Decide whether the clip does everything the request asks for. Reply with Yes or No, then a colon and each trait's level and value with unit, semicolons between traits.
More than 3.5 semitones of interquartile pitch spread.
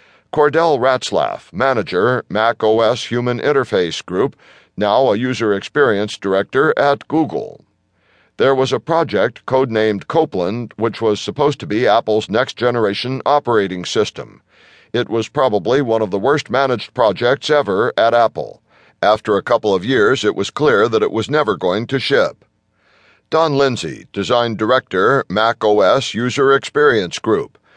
Yes: average, 4.9 semitones